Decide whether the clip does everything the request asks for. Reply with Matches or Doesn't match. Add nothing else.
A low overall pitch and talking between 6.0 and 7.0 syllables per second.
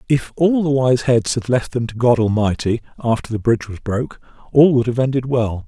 Doesn't match